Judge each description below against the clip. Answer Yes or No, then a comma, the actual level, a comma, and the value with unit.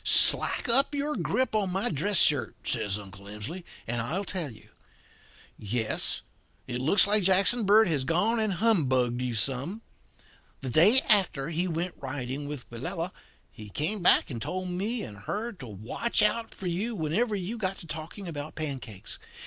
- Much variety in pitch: Yes, wide, 8.0 semitones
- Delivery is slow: No, average, 170 wpm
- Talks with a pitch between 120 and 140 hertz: No, medium, 170 Hz